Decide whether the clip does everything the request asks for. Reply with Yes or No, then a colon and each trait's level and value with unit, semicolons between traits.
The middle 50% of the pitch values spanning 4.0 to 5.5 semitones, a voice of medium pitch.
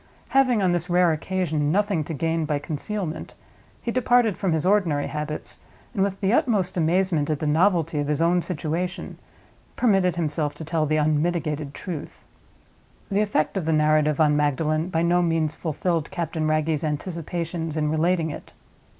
No: average, 3.1 semitones; medium, 165 Hz